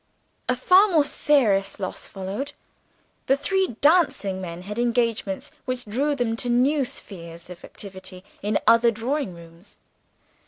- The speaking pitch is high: Yes, high, 230 Hz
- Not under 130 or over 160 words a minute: Yes, slow, 135 wpm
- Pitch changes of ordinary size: No, wide, 6.4 semitones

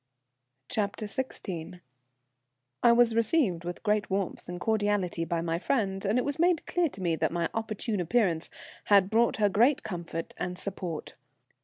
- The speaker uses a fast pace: No, average, 155 wpm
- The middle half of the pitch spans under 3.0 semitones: No, average, 4.7 semitones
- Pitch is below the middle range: No, high, 205 Hz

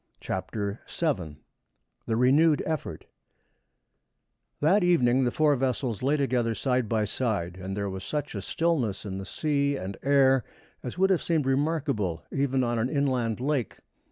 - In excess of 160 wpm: No, average, 155 wpm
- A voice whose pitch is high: No, low, 130 Hz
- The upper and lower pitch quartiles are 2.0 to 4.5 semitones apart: No, average, 5.1 semitones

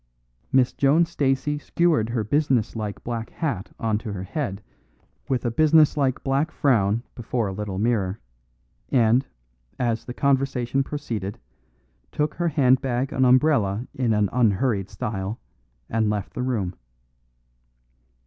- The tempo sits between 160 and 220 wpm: No, slow, 135 wpm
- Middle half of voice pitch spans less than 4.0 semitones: No, average, 4.4 semitones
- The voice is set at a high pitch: No, low, 120 Hz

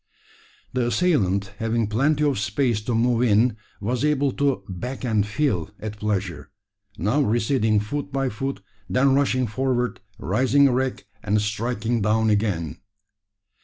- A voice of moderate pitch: No, low, 115 Hz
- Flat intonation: No, average, 4.1 semitones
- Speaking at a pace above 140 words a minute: No, slow, 135 wpm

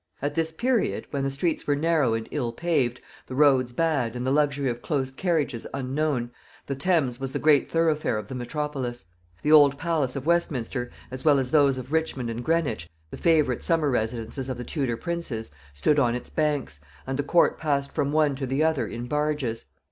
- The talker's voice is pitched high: No, medium, 140 Hz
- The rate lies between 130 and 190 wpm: No, average, 200 wpm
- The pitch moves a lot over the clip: No, average, 3.8 semitones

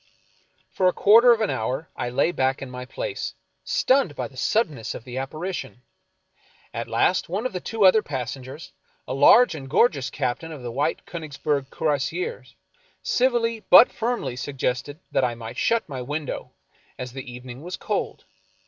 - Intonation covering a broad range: Yes, wide, 6.9 semitones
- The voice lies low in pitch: No, medium, 145 Hz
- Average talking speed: Yes, average, 165 wpm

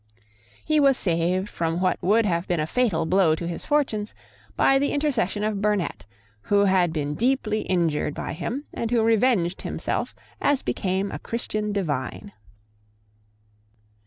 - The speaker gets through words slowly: No, average, 150 wpm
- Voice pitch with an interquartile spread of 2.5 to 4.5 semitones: No, average, 5.1 semitones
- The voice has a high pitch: Yes, high, 200 Hz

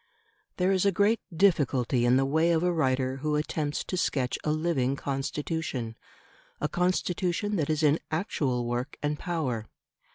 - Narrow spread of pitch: No, average, 4.7 semitones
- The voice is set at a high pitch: No, medium, 150 Hz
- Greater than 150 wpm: Yes, average, 160 wpm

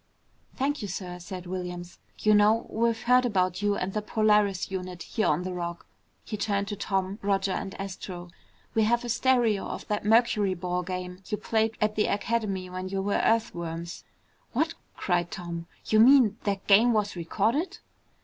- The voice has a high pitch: Yes, high, 200 Hz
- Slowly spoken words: No, average, 170 wpm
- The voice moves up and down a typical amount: Yes, average, 3.4 semitones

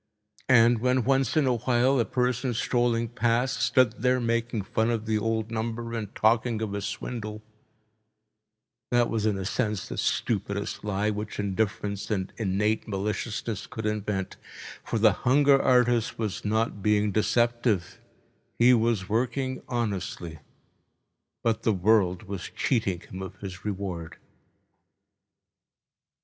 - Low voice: Yes, low, 110 Hz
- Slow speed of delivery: Yes, slow, 130 wpm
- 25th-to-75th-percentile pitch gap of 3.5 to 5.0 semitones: No, average, 2.7 semitones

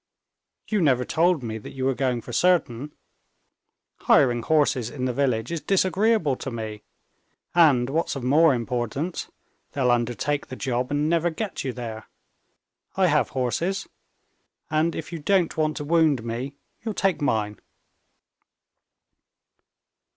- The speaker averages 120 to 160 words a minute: Yes, average, 140 wpm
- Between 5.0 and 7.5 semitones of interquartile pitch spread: Yes, average, 5.3 semitones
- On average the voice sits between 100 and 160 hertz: Yes, medium, 140 Hz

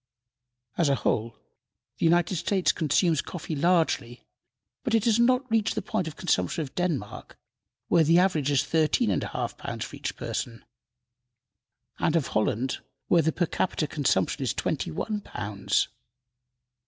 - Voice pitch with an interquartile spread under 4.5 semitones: No, average, 5.0 semitones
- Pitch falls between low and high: Yes, medium, 160 Hz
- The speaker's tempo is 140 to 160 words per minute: Yes, average, 155 wpm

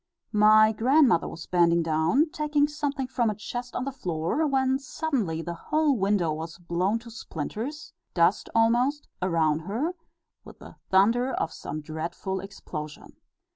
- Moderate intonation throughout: No, wide, 7.8 semitones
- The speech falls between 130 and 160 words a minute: Yes, average, 145 wpm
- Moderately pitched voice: No, high, 215 Hz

